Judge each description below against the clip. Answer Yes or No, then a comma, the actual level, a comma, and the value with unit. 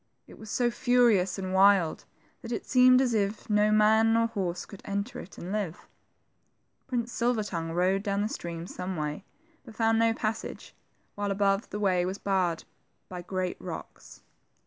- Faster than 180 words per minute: No, average, 175 wpm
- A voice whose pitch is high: Yes, high, 205 Hz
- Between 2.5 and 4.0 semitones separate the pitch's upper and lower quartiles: Yes, average, 3.4 semitones